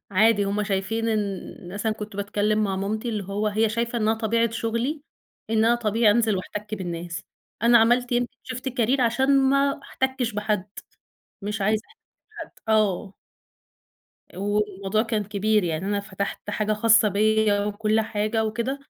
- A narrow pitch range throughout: Yes, narrow, 2.0 semitones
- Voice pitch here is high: Yes, high, 215 Hz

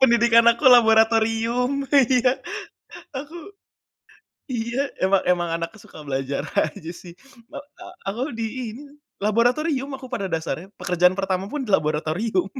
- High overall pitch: Yes, high, 225 Hz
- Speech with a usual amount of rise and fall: No, wide, 5.7 semitones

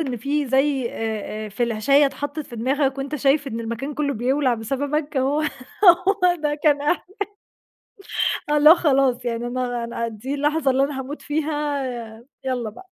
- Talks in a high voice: Yes, very high, 275 Hz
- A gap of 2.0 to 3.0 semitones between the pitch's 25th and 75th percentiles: No, average, 3.4 semitones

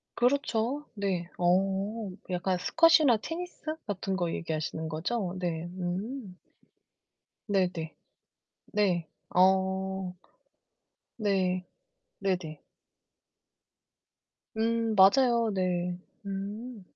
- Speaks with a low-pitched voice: No, high, 190 Hz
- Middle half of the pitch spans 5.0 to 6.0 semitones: No, average, 4.0 semitones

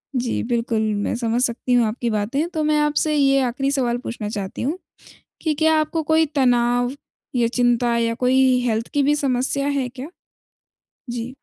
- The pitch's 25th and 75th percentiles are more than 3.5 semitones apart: No, average, 3.2 semitones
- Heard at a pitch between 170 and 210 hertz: No, very high, 250 Hz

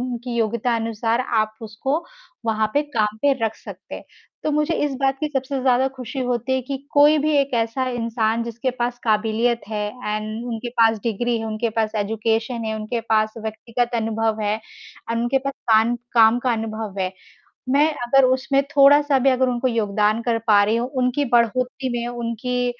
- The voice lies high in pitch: Yes, high, 235 Hz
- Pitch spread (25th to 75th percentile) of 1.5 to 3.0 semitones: Yes, average, 2.7 semitones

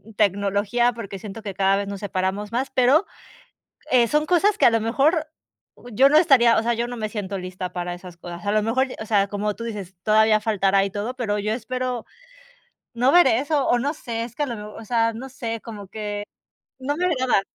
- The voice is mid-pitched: No, high, 225 Hz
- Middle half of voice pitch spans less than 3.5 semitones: No, average, 3.9 semitones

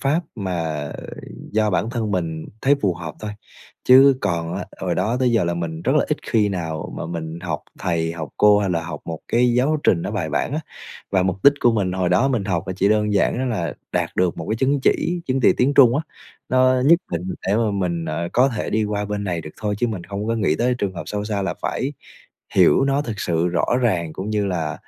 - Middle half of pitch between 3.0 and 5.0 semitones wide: No, wide, 5.5 semitones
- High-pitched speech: No, low, 100 Hz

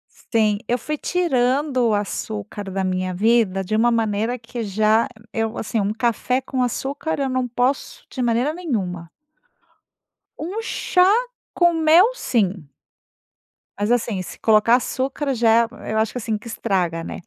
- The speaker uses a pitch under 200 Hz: No, high, 230 Hz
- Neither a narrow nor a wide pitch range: Yes, average, 3.9 semitones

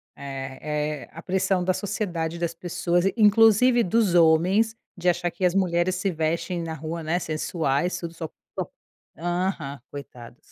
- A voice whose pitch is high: No, medium, 170 Hz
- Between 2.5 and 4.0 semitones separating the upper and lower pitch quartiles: Yes, average, 2.8 semitones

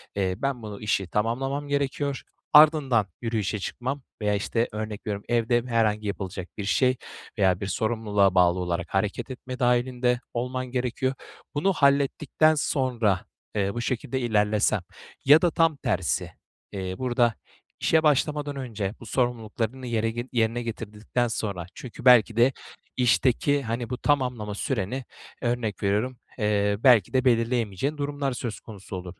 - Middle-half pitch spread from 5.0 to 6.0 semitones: No, average, 3.8 semitones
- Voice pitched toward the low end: Yes, low, 120 Hz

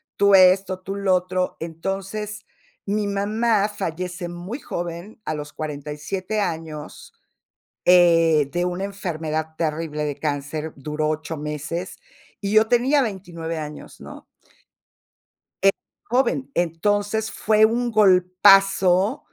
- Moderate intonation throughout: Yes, average, 4.2 semitones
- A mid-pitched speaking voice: Yes, medium, 180 Hz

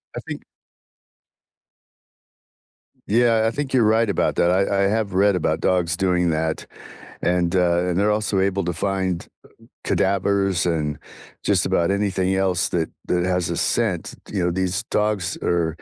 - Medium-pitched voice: No, very low, 95 Hz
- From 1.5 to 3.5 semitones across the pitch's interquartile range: Yes, narrow, 2.4 semitones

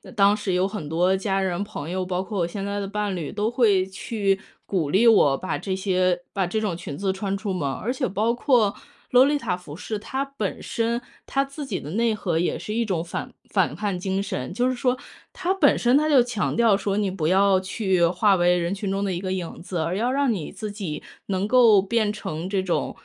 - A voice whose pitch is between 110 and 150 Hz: No, high, 200 Hz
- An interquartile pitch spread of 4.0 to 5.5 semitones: No, average, 3.6 semitones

